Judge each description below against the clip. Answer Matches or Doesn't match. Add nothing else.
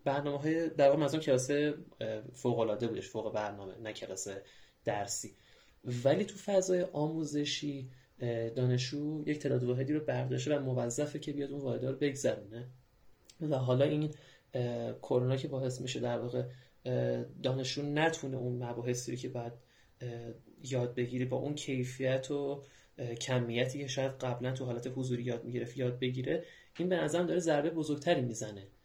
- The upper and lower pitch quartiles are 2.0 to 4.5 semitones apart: Matches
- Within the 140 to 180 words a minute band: Matches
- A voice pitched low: Matches